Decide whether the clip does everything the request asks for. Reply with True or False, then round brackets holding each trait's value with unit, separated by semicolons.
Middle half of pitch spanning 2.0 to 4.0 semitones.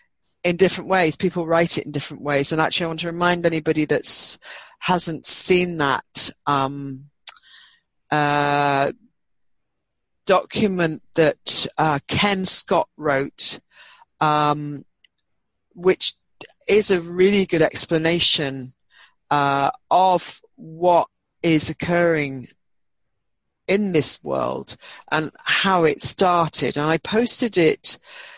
True (3.6 semitones)